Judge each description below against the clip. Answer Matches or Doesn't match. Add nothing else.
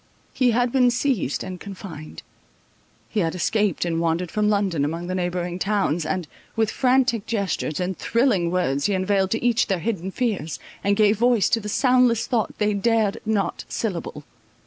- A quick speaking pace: Doesn't match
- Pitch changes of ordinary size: Matches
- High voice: Matches